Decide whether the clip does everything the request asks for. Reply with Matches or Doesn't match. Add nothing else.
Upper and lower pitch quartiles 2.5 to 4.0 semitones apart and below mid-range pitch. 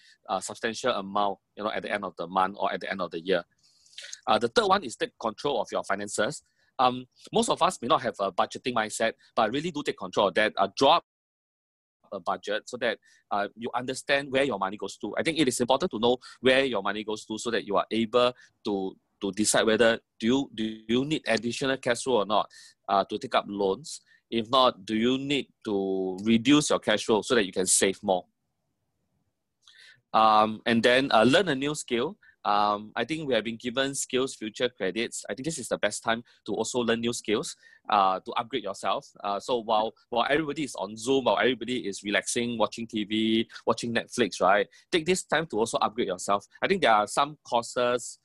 Matches